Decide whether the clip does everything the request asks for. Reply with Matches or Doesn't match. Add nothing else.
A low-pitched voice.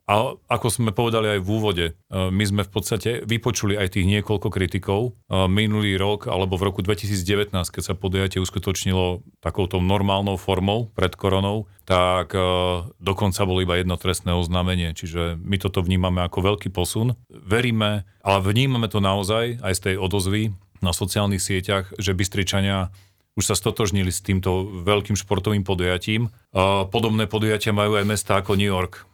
Matches